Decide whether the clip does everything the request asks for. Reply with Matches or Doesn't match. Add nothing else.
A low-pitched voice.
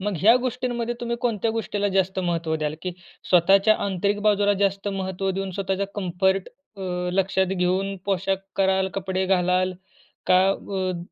Doesn't match